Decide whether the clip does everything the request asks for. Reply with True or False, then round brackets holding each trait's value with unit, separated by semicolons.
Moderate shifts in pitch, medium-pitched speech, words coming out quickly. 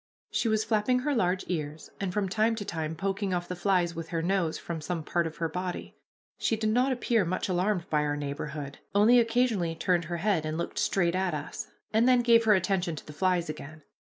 True (4.5 semitones; 180 Hz; 220 wpm)